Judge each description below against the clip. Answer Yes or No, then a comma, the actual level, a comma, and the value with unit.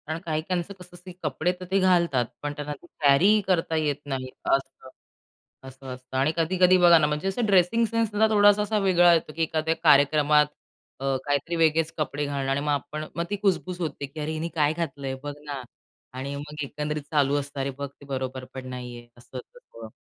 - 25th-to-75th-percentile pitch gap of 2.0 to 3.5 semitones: No, average, 4.0 semitones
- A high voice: No, medium, 150 Hz